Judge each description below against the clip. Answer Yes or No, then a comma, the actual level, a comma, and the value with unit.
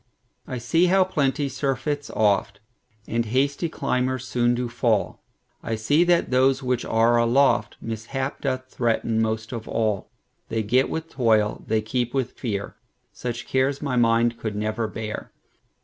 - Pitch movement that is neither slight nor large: Yes, average, 3.1 semitones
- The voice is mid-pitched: No, low, 120 Hz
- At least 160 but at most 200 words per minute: No, slow, 135 wpm